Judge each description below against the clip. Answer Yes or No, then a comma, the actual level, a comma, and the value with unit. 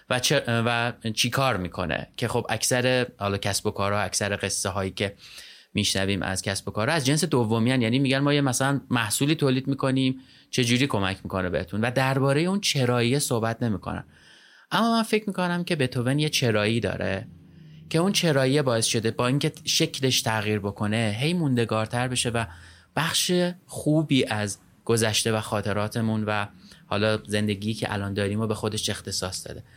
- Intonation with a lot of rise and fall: No, average, 4.6 semitones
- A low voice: Yes, low, 115 Hz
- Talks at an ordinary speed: No, fast, 170 wpm